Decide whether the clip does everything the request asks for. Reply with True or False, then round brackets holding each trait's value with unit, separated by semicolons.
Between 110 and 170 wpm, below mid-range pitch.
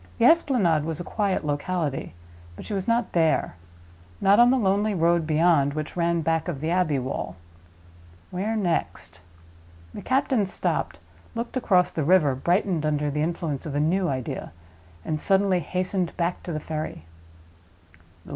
False (155 wpm; 170 Hz)